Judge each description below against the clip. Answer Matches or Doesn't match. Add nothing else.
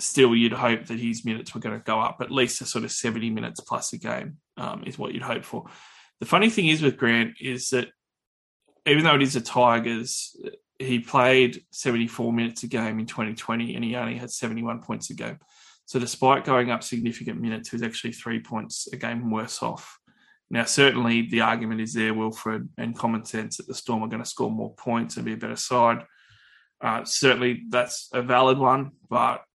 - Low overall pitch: Matches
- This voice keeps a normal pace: Doesn't match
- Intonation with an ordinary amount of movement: Doesn't match